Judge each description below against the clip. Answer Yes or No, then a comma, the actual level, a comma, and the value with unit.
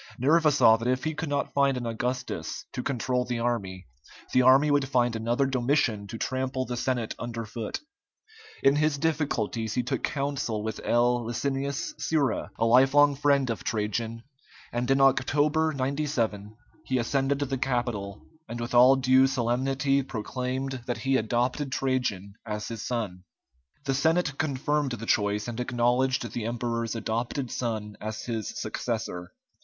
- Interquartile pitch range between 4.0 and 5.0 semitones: No, average, 2.9 semitones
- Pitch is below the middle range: Yes, low, 125 Hz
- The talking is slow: No, average, 155 wpm